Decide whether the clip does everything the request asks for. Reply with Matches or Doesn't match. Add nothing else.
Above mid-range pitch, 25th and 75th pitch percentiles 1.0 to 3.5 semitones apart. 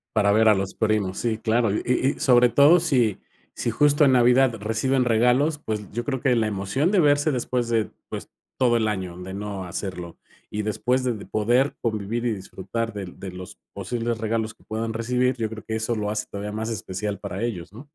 Doesn't match